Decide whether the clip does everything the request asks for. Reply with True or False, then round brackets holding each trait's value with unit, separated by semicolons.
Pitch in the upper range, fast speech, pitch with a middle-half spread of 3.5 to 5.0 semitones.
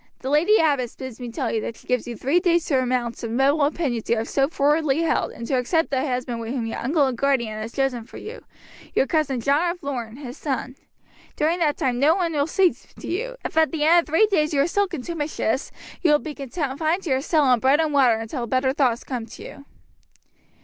True (275 Hz; 235 wpm; 4.3 semitones)